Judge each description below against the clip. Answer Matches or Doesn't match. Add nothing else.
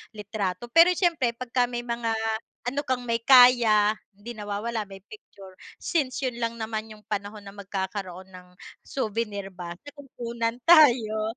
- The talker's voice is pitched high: Matches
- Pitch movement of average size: Matches